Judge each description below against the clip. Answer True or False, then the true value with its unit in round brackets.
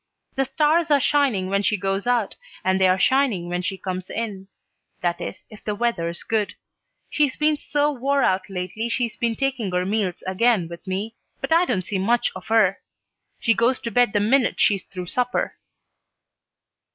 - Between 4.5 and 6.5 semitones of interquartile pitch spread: True (4.8 semitones)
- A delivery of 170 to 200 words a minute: True (180 wpm)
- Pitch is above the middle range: True (215 Hz)